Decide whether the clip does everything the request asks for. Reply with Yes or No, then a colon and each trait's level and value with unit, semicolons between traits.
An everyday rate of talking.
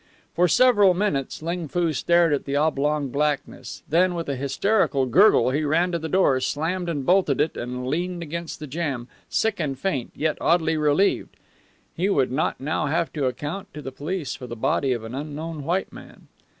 Yes: average, 190 wpm